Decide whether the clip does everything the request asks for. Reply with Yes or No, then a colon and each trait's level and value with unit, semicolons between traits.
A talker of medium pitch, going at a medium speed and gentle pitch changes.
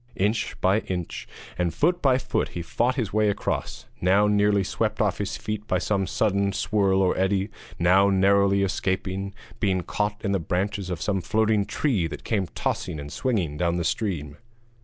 No: low, 100 Hz; average, 180 wpm; narrow, 2.1 semitones